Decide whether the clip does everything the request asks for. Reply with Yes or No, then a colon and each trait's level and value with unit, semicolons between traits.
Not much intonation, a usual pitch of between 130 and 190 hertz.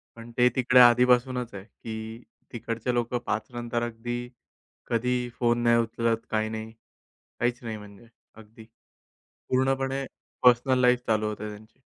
No: narrow, 1.8 semitones; low, 120 Hz